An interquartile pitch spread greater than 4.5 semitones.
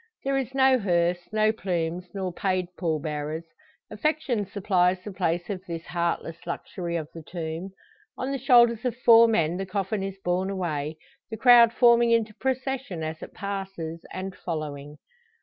Yes: average, 5.2 semitones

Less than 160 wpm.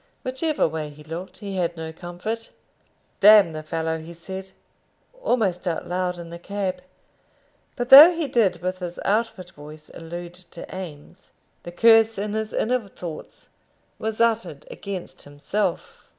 Yes: average, 150 wpm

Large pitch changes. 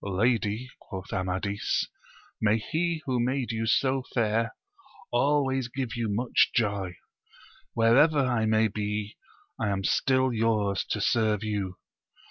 No: average, 3.7 semitones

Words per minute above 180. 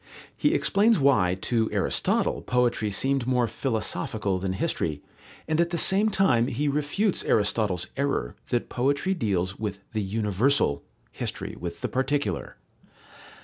No: slow, 135 wpm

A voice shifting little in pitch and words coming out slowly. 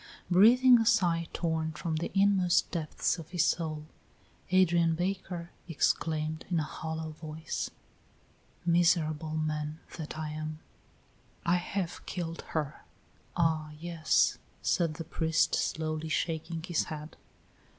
Yes: narrow, 1.9 semitones; slow, 120 wpm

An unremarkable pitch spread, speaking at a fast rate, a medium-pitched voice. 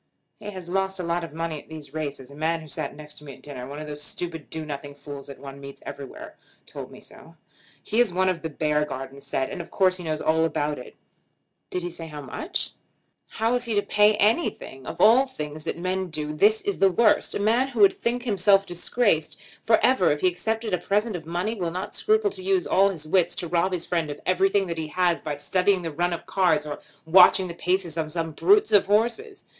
Yes: average, 5.0 semitones; fast, 235 wpm; medium, 175 Hz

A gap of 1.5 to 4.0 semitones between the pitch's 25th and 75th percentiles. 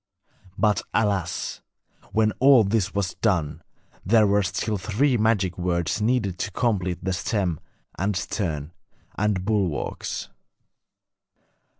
Yes: average, 3.2 semitones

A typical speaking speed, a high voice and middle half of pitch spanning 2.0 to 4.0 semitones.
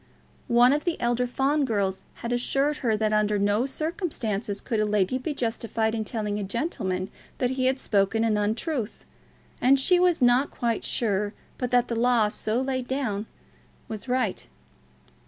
Yes: average, 170 wpm; high, 235 Hz; average, 3.7 semitones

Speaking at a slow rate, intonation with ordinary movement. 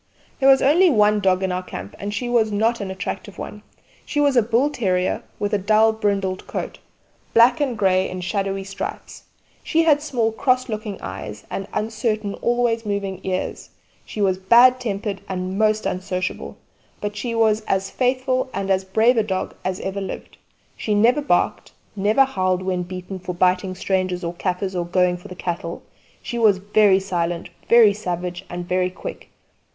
No: average, 180 wpm; average, 3.5 semitones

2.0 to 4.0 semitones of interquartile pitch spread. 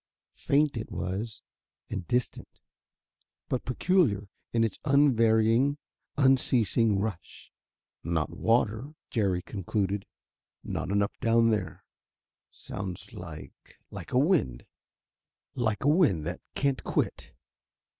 No: average, 5.1 semitones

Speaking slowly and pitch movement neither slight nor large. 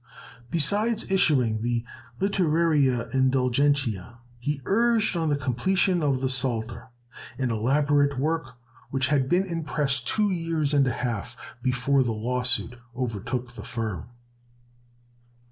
Yes: slow, 125 wpm; average, 4.6 semitones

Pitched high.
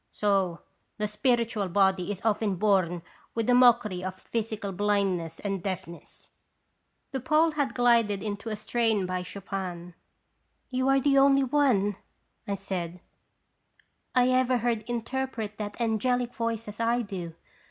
Yes: high, 210 Hz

